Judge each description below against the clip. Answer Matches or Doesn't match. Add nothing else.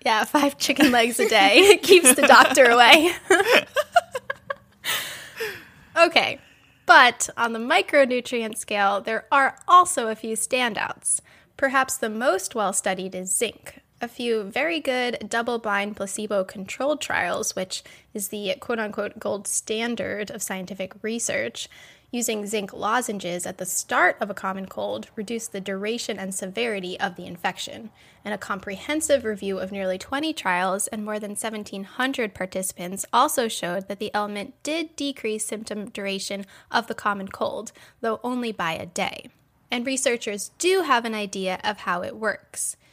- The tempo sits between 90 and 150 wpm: Matches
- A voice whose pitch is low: Doesn't match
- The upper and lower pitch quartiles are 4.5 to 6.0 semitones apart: Matches